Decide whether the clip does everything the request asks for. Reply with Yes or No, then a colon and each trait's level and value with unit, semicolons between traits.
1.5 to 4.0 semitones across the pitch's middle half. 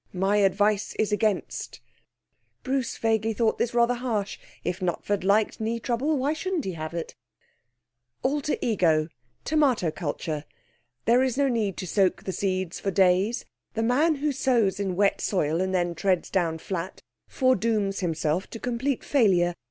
No: average, 4.9 semitones